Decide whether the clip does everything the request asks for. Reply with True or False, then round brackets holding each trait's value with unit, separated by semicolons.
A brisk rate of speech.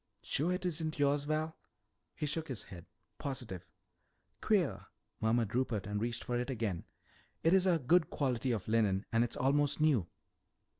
False (155 wpm)